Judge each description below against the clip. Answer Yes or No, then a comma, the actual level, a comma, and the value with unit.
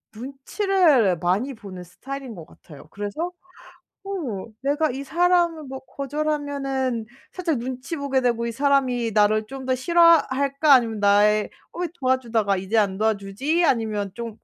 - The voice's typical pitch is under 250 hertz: No, very high, 260 Hz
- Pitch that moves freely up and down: No, average, 5.0 semitones